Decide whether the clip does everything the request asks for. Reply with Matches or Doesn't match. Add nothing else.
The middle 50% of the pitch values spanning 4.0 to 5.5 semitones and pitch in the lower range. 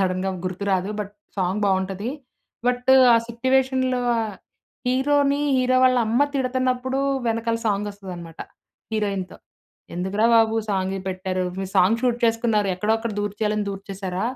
Doesn't match